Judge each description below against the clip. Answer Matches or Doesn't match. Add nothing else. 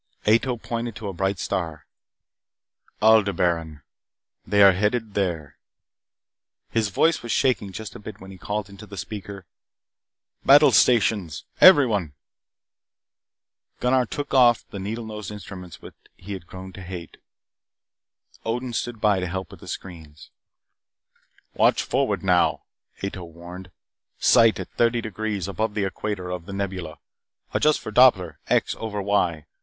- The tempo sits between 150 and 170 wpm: Doesn't match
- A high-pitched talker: Doesn't match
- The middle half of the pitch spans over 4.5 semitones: Doesn't match